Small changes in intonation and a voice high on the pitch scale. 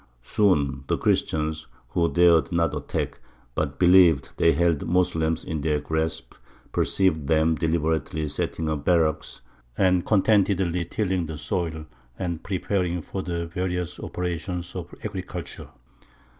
No: narrow, 2.3 semitones; very low, 85 Hz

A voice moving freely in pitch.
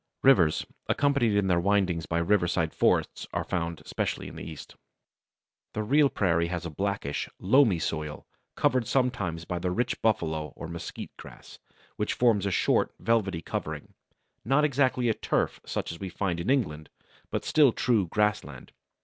Yes: wide, 5.7 semitones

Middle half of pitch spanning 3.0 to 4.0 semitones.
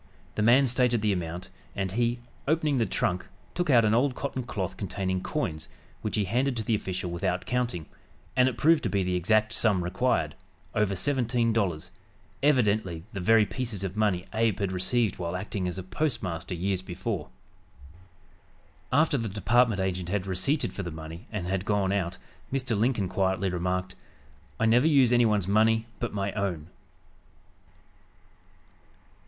No: average, 4.5 semitones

